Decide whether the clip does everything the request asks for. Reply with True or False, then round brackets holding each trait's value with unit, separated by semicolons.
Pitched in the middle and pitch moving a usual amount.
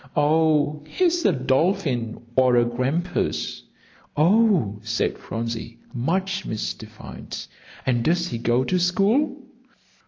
False (150 Hz; 7.3 semitones)